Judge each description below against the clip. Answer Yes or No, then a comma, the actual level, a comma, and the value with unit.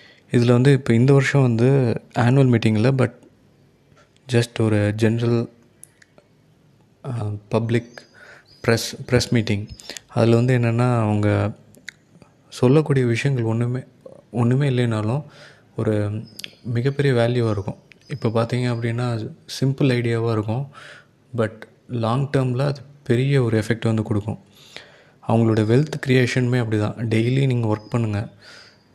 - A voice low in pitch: Yes, low, 120 Hz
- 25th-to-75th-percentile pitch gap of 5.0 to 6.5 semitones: No, average, 3.1 semitones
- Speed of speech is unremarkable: Yes, average, 110 wpm